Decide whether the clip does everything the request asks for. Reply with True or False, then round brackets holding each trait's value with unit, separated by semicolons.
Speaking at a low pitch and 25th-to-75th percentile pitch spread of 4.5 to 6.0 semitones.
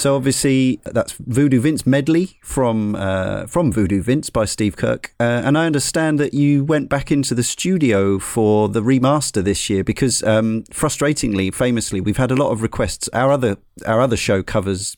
True (125 Hz; 5.0 semitones)